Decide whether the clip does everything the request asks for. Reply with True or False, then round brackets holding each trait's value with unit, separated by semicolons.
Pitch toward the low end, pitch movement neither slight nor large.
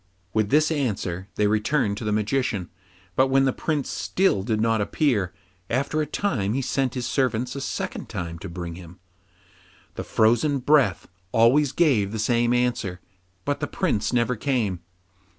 True (120 Hz; 4.8 semitones)